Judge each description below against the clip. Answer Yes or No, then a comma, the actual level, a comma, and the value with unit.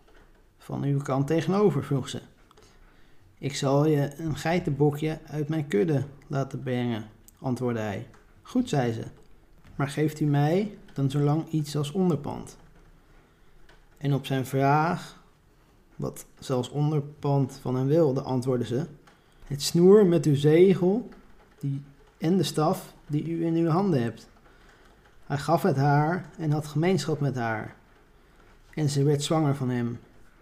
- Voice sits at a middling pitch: Yes, medium, 145 Hz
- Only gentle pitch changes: No, average, 3.5 semitones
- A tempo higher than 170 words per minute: No, average, 140 wpm